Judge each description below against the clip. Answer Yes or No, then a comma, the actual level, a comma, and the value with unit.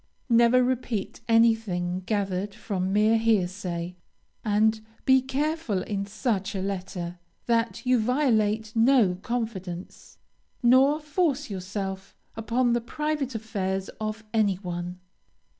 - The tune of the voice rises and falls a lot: No, average, 4.0 semitones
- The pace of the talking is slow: Yes, slow, 110 wpm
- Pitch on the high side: Yes, high, 220 Hz